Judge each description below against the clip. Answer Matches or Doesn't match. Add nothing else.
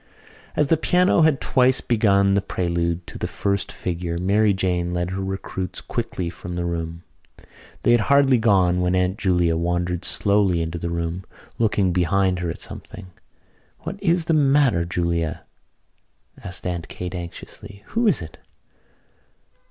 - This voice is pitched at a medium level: Doesn't match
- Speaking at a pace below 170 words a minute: Matches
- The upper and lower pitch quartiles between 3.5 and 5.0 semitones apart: Matches